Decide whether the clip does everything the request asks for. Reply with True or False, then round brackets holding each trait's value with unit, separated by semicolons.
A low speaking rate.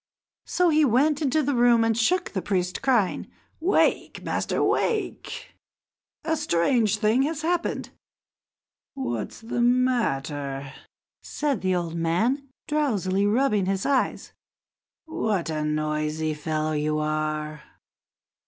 True (115 wpm)